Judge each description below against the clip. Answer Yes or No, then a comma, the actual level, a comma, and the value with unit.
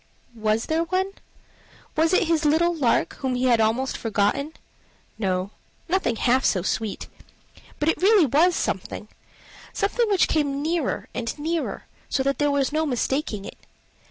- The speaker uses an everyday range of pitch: No, wide, 6.0 semitones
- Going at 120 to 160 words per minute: Yes, average, 155 wpm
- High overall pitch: Yes, very high, 285 Hz